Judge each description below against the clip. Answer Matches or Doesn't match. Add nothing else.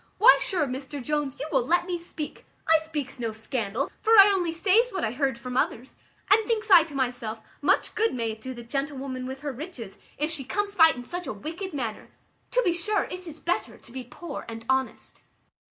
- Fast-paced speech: Matches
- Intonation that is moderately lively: Doesn't match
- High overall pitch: Matches